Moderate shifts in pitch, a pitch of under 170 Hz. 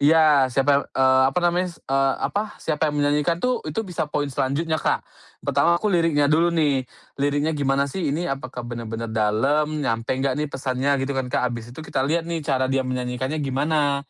Yes: average, 3.1 semitones; medium, 140 Hz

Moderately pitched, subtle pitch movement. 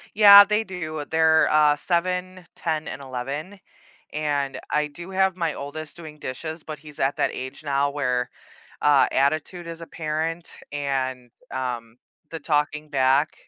No: medium, 150 Hz; average, 3.1 semitones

